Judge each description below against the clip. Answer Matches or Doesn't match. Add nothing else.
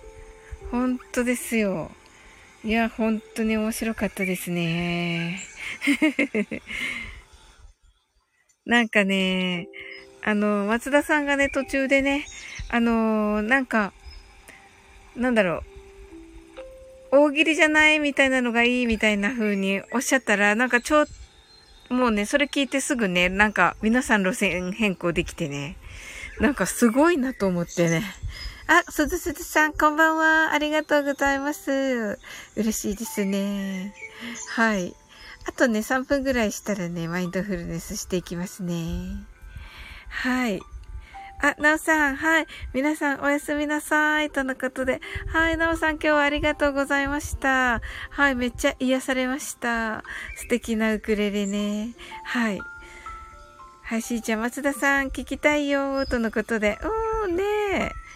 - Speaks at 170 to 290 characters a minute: Matches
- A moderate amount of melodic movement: Doesn't match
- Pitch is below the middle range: Doesn't match